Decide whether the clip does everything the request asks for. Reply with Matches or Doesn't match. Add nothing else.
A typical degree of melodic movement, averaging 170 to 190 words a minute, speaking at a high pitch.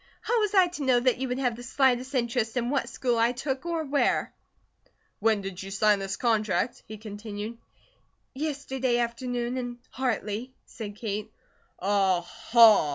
Doesn't match